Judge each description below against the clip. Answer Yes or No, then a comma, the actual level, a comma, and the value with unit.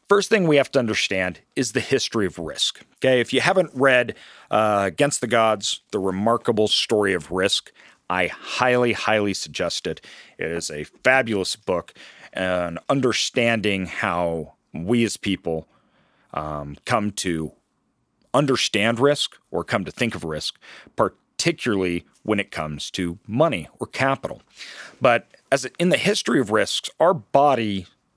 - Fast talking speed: No, average, 145 wpm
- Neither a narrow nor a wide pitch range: No, wide, 6.4 semitones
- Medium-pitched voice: No, low, 110 Hz